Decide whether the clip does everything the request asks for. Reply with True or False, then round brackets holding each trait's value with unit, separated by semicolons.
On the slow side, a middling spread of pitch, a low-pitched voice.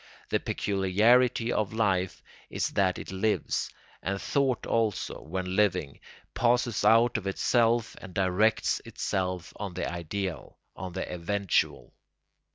True (125 wpm; 3.5 semitones; 100 Hz)